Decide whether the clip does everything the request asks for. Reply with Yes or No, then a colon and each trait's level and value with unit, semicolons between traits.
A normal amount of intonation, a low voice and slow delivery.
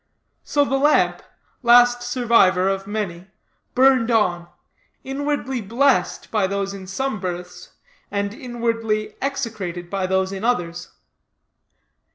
No: average, 4.6 semitones; high, 215 Hz; slow, 115 wpm